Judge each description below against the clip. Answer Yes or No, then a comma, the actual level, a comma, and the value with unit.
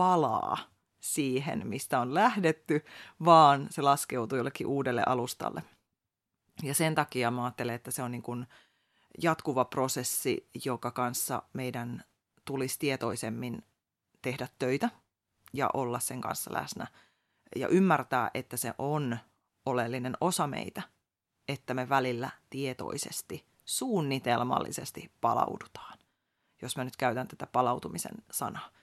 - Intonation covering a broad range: No, average, 2.7 semitones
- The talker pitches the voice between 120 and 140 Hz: Yes, low, 130 Hz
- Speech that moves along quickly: No, average, 115 wpm